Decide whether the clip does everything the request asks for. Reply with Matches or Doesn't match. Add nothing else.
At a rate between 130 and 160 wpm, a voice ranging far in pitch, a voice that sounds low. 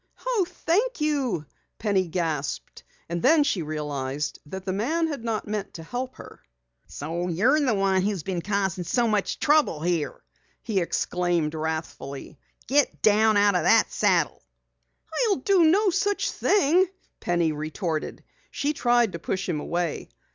Doesn't match